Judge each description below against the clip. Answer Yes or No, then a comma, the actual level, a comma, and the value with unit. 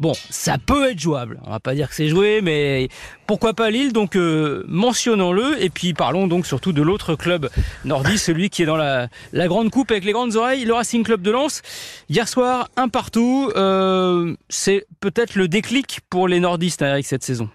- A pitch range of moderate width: No, wide, 6.0 semitones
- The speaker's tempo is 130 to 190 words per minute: No, average, 205 wpm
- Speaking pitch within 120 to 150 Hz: No, high, 190 Hz